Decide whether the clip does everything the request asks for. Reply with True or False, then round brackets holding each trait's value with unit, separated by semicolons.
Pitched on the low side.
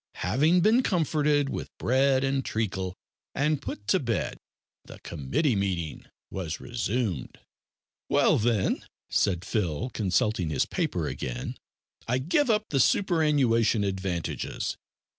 True (120 Hz)